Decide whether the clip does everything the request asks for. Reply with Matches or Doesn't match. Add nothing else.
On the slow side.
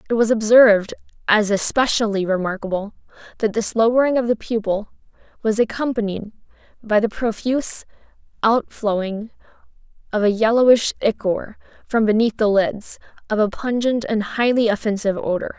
Matches